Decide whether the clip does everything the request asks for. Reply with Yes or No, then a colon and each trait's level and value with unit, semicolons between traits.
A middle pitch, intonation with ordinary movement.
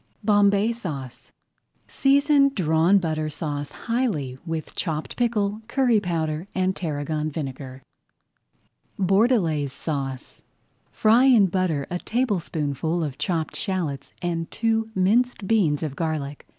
No: medium, 175 Hz; wide, 6.1 semitones